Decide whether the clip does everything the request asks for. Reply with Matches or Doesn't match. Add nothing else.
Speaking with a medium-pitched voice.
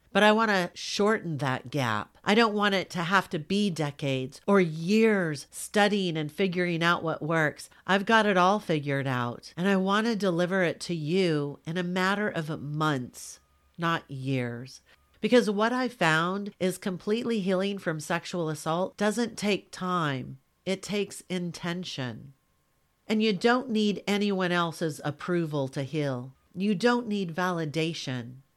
Matches